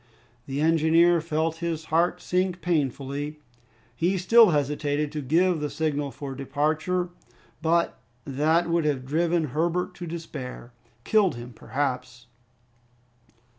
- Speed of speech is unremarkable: No, slow, 120 wpm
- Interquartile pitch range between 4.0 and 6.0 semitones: No, average, 3.1 semitones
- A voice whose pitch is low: No, medium, 155 Hz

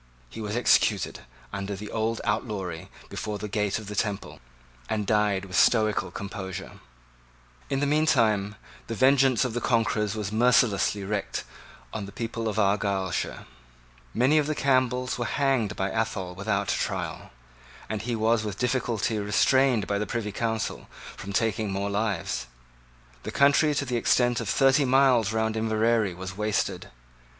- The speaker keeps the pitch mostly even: No, average, 3.2 semitones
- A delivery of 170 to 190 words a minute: No, average, 155 wpm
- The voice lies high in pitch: No, low, 110 Hz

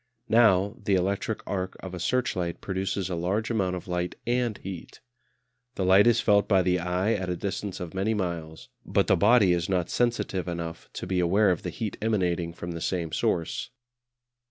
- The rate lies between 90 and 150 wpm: No, average, 190 wpm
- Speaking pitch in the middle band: No, very low, 95 Hz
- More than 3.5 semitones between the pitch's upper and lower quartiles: No, narrow, 2.5 semitones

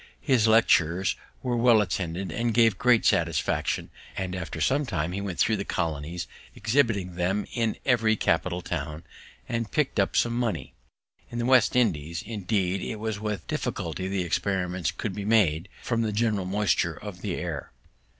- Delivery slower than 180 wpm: Yes, average, 170 wpm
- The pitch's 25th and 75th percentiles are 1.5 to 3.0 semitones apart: No, average, 4.4 semitones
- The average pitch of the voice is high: No, low, 100 Hz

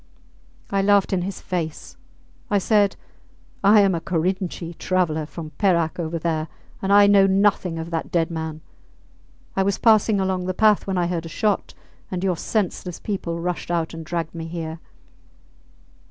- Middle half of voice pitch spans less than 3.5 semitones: Yes, average, 3.0 semitones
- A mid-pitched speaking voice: Yes, medium, 180 Hz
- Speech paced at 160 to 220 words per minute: Yes, average, 165 wpm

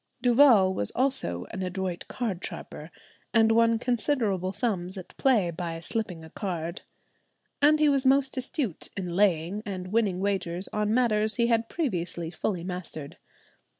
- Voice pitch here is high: Yes, high, 200 Hz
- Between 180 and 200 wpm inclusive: No, average, 150 wpm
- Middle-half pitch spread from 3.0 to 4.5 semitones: No, average, 5.0 semitones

